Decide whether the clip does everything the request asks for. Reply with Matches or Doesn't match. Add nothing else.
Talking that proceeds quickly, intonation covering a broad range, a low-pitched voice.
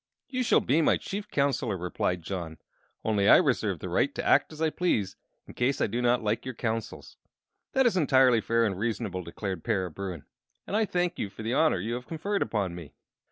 Matches